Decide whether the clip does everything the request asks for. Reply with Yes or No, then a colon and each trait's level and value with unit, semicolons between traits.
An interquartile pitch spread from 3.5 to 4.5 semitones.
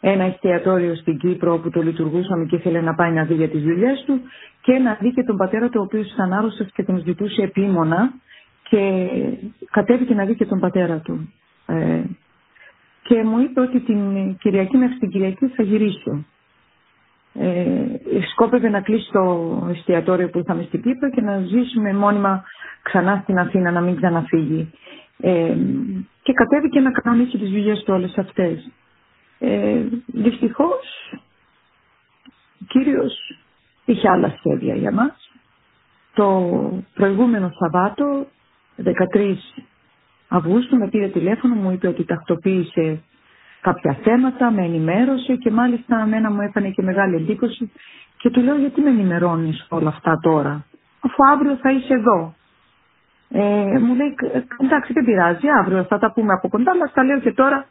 No: wide, 5.4 semitones